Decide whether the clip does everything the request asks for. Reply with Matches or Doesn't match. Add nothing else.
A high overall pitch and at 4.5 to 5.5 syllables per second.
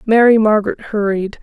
Matches